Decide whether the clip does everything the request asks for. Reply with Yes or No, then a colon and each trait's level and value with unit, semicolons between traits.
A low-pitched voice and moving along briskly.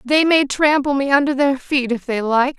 No: very high, 275 Hz; fast, 230 wpm